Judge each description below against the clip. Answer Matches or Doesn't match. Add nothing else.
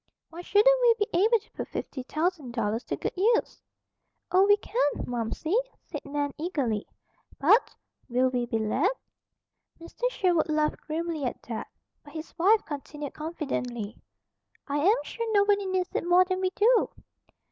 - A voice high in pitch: Matches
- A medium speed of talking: Matches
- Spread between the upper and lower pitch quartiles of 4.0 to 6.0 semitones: Doesn't match